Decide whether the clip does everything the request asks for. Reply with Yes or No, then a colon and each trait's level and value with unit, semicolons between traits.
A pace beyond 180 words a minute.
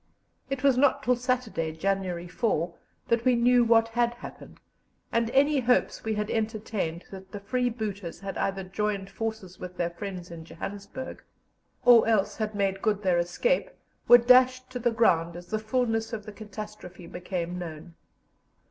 No: average, 165 wpm